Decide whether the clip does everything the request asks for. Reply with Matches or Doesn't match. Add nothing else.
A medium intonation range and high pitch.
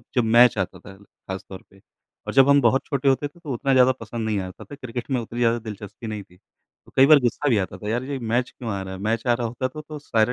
Doesn't match